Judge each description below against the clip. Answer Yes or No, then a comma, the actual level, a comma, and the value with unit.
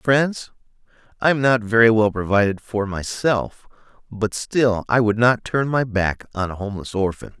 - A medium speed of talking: Yes, average, 170 wpm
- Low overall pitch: Yes, low, 110 Hz